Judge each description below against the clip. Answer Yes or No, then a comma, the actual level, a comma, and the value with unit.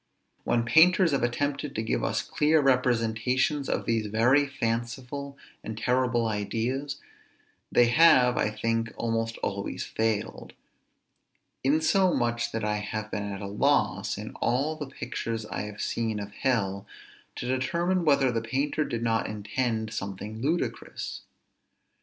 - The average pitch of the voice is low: Yes, low, 120 Hz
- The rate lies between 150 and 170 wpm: No, slow, 135 wpm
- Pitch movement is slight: No, average, 3.9 semitones